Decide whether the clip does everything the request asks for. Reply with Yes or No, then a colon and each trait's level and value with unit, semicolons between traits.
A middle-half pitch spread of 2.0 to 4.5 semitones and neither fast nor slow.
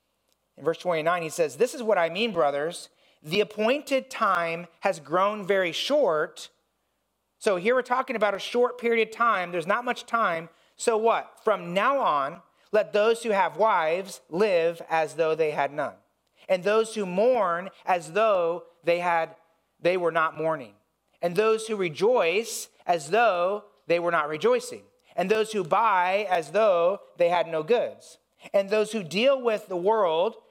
No: average, 5.1 semitones; average, 170 wpm